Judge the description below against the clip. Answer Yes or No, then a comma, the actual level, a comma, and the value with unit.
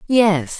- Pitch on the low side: No, high, 195 Hz